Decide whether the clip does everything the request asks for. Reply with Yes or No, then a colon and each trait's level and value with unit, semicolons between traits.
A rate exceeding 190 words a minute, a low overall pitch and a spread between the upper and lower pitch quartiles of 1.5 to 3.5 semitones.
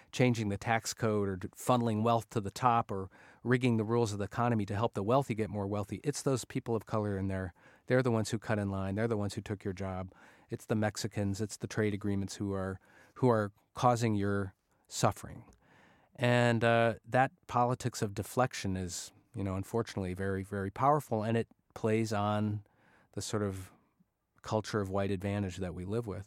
Yes: average, 200 wpm; low, 105 Hz; average, 2.9 semitones